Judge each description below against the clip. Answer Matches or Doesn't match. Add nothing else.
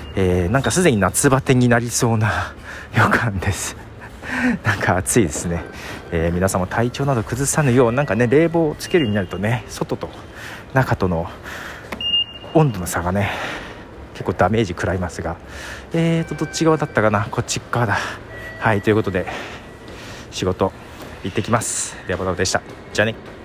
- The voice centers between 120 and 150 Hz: Doesn't match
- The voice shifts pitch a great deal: Doesn't match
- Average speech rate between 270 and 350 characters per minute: Matches